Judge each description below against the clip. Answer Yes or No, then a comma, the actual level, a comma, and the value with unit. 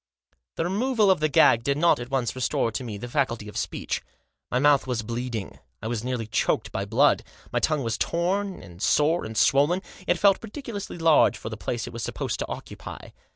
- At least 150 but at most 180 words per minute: No, fast, 205 wpm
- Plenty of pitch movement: Yes, wide, 6.8 semitones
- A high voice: No, low, 135 Hz